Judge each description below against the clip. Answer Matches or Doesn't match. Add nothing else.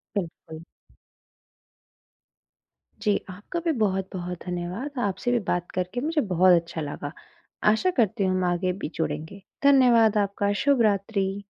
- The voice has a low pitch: Doesn't match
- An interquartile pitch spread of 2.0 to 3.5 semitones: Doesn't match